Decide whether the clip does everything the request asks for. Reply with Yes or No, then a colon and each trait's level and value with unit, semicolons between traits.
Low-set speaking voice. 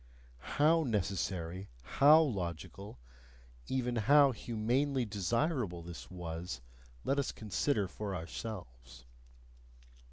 Yes: low, 105 Hz